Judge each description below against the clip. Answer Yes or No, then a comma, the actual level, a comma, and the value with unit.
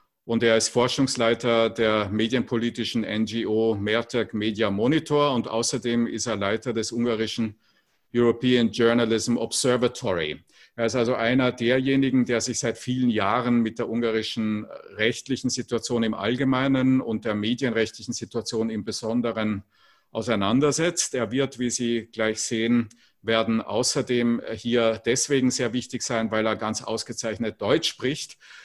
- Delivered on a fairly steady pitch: Yes, narrow, 1.7 semitones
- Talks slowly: Yes, slow, 130 wpm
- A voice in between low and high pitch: No, low, 115 Hz